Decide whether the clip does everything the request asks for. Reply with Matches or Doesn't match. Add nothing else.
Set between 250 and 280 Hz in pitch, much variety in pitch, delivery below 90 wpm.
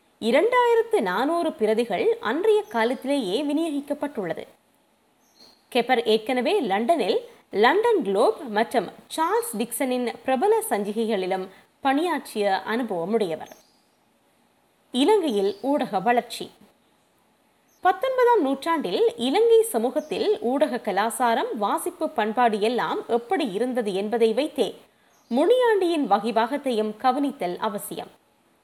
Matches